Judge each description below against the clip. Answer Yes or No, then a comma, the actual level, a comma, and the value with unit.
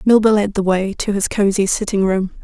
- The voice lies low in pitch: No, high, 200 Hz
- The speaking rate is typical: No, fast, 220 wpm